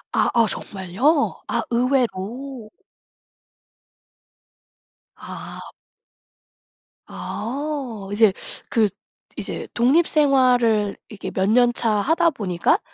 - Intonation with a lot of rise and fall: No, average, 4.8 semitones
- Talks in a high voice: Yes, high, 235 Hz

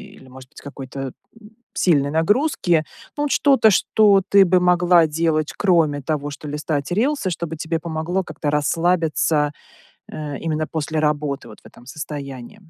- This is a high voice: No, medium, 160 Hz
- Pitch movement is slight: No, average, 3.5 semitones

